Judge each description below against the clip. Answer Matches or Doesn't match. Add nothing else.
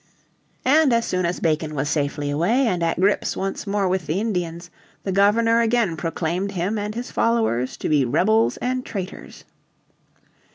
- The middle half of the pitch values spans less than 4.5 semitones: Doesn't match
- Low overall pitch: Doesn't match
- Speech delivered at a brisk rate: Doesn't match